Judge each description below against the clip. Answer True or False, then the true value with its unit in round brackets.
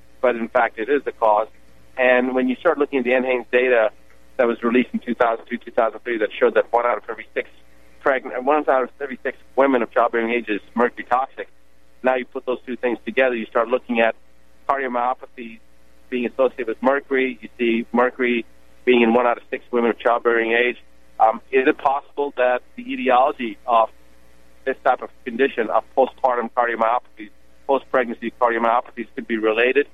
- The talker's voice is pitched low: True (120 Hz)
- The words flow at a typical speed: True (180 wpm)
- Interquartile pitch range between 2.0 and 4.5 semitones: True (3.4 semitones)